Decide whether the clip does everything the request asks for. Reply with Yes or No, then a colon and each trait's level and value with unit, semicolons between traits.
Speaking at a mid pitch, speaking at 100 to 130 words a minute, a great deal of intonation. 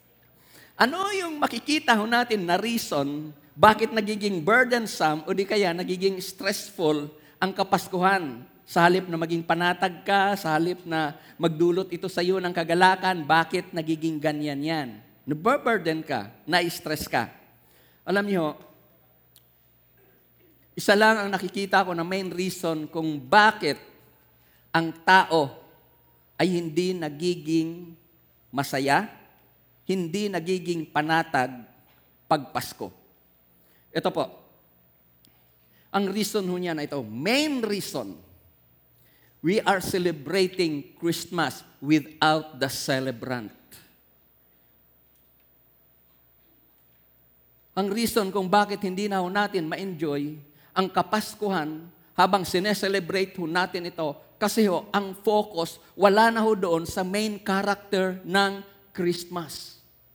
No: medium, 175 Hz; slow, 110 wpm; average, 4.3 semitones